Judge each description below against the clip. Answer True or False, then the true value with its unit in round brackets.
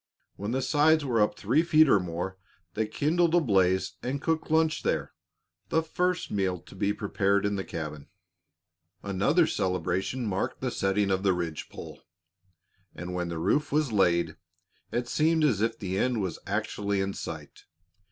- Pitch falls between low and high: False (105 Hz)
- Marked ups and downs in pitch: True (7.6 semitones)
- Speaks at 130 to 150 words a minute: False (170 wpm)